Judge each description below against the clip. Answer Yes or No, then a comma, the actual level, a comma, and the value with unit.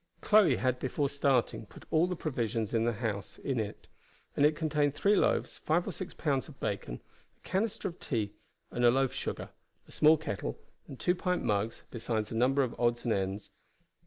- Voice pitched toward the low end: Yes, low, 130 Hz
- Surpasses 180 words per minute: Yes, average, 190 wpm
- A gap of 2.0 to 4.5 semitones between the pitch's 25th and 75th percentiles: No, wide, 5.6 semitones